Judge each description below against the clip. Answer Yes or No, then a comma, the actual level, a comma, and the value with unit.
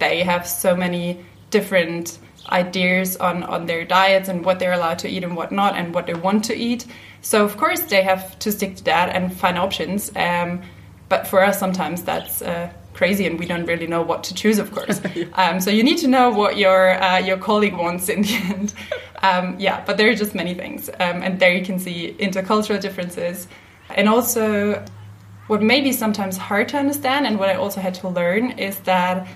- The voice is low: No, high, 190 Hz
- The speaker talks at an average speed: No, fast, 215 wpm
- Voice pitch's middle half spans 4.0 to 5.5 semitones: No, narrow, 2.6 semitones